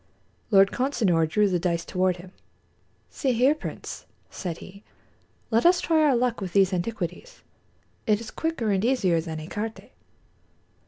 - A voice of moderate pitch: No, high, 205 Hz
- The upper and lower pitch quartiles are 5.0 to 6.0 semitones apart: Yes, wide, 5.5 semitones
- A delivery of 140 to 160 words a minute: Yes, average, 150 wpm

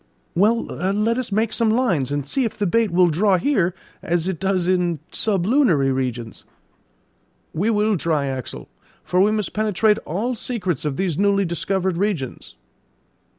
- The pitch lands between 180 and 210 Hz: Yes, high, 190 Hz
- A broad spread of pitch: No, average, 4.2 semitones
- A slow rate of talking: No, average, 155 wpm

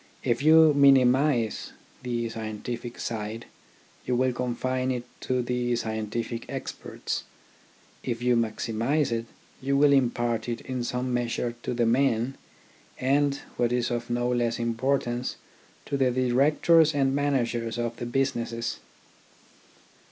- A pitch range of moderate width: No, narrow, 2.2 semitones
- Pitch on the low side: Yes, low, 120 Hz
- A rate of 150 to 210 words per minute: No, slow, 135 wpm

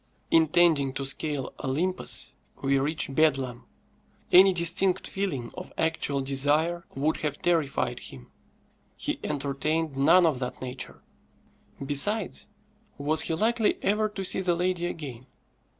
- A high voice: No, medium, 155 Hz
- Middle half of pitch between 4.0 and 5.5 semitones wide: Yes, average, 4.3 semitones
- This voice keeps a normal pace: No, slow, 125 wpm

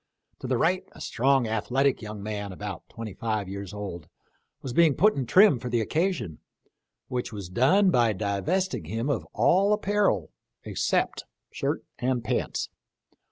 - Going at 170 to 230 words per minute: No, average, 155 wpm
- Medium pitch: No, low, 120 Hz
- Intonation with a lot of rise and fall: Yes, wide, 7.4 semitones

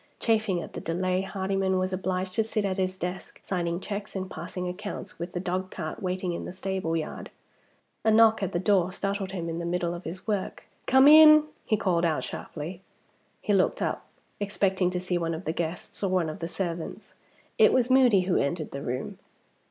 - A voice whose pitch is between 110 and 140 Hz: No, medium, 185 Hz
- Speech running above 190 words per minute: Yes, average, 200 wpm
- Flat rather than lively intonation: Yes, narrow, 2.3 semitones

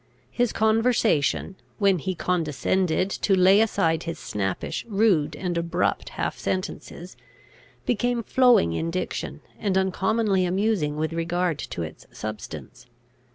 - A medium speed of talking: No, slow, 120 wpm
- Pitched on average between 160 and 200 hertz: Yes, medium, 185 Hz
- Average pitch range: Yes, average, 4.2 semitones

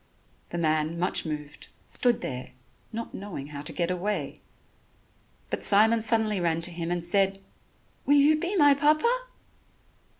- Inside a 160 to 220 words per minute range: No, average, 145 wpm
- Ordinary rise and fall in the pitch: No, wide, 6.5 semitones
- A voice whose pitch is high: Yes, high, 195 Hz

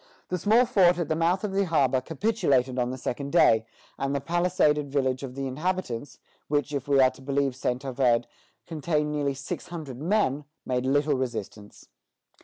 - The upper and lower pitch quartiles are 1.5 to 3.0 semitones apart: No, average, 4.4 semitones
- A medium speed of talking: Yes, average, 180 wpm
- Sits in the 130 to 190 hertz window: Yes, medium, 140 Hz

